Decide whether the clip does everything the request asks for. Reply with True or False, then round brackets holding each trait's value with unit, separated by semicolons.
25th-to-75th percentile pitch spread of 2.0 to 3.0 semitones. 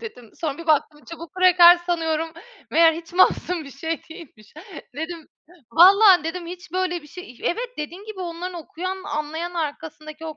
True (2.7 semitones)